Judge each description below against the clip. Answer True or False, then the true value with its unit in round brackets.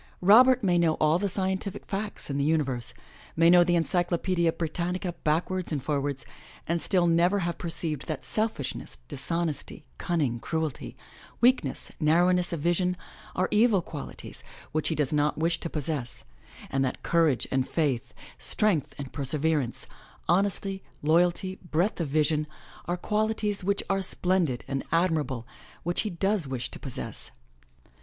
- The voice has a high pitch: False (170 Hz)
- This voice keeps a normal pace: True (150 wpm)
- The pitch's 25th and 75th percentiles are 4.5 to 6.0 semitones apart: False (3.7 semitones)